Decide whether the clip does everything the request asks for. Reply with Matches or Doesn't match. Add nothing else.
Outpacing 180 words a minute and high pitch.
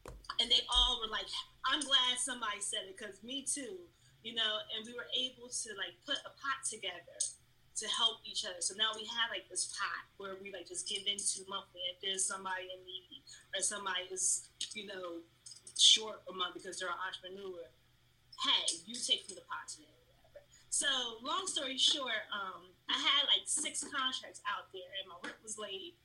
Matches